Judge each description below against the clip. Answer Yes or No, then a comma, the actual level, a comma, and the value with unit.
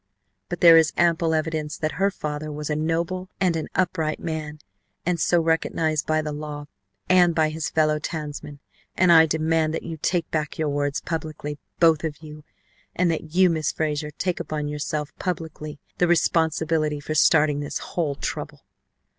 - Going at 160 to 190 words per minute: Yes, average, 170 wpm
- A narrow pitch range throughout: Yes, narrow, 1.7 semitones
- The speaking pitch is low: No, medium, 155 Hz